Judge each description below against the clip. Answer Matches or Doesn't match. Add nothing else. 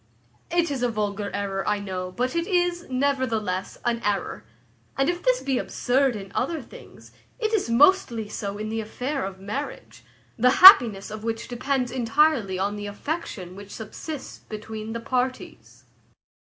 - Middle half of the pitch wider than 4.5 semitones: Matches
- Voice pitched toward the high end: Matches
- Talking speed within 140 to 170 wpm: Matches